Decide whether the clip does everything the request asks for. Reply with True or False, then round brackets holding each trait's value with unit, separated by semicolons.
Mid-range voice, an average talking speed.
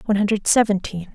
False (205 Hz; 155 wpm)